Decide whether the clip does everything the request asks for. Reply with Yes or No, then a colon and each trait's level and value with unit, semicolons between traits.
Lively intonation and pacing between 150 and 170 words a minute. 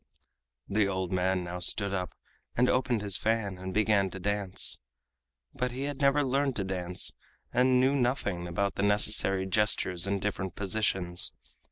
No: average, 4.5 semitones; average, 160 wpm